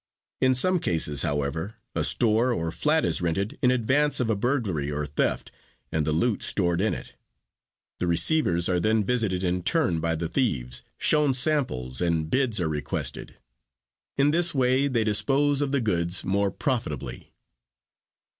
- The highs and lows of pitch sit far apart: Yes, wide, 7.8 semitones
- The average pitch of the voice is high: No, low, 105 Hz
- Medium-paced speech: Yes, average, 160 wpm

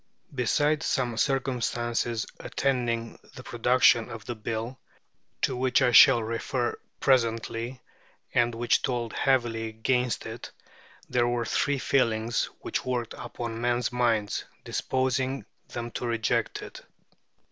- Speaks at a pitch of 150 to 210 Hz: No, low, 120 Hz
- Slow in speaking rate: Yes, slow, 120 wpm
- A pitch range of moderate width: No, narrow, 1.8 semitones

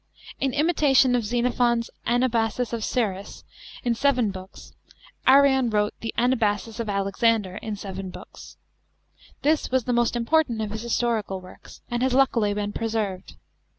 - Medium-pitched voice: No, high, 230 Hz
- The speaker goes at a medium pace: Yes, average, 150 wpm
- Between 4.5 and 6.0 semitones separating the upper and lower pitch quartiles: No, average, 3.2 semitones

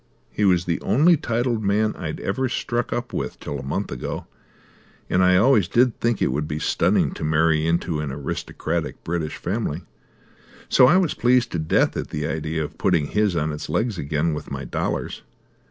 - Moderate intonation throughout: No, wide, 7.4 semitones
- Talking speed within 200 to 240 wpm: No, average, 185 wpm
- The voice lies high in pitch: No, very low, 90 Hz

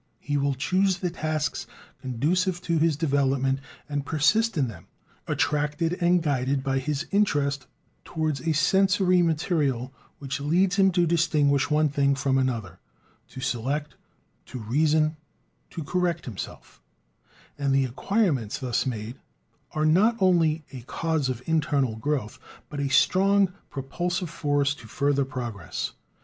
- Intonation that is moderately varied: Yes, average, 3.9 semitones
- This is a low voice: No, medium, 145 Hz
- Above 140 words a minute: No, slow, 135 wpm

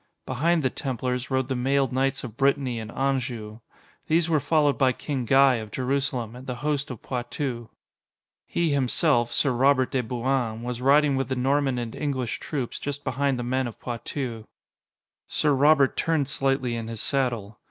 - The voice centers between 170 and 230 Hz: No, low, 130 Hz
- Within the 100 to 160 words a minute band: No, average, 175 wpm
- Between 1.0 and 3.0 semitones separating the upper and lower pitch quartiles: Yes, narrow, 2.5 semitones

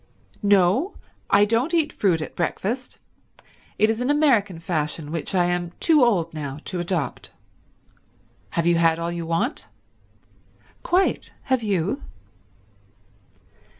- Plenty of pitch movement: Yes, wide, 6.3 semitones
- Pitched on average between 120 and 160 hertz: No, medium, 185 Hz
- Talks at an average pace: No, slow, 125 wpm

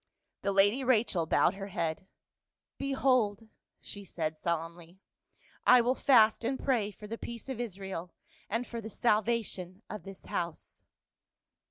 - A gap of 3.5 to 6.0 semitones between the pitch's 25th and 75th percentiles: Yes, average, 4.5 semitones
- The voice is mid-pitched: No, high, 210 Hz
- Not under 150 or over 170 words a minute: Yes, average, 155 wpm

